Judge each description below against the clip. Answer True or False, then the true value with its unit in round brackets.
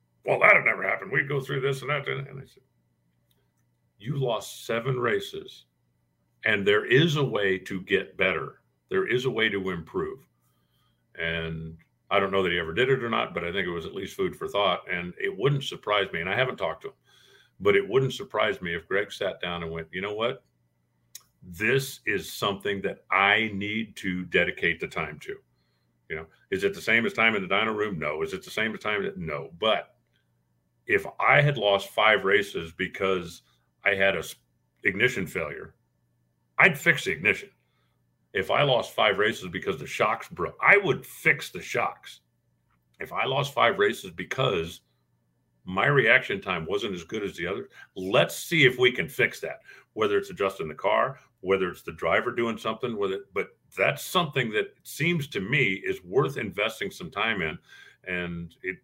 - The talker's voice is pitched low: True (95 Hz)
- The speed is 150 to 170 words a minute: False (195 wpm)